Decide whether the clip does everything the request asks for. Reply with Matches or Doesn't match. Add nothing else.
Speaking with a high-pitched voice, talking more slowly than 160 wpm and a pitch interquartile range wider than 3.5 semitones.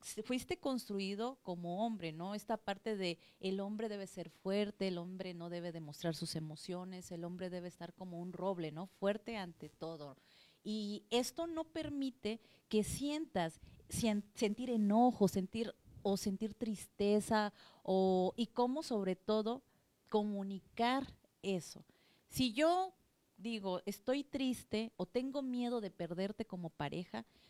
Matches